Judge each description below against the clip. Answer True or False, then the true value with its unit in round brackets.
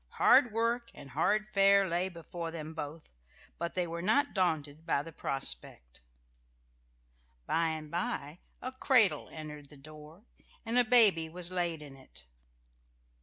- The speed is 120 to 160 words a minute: True (145 wpm)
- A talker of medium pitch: True (170 Hz)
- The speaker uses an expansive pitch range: False (4.6 semitones)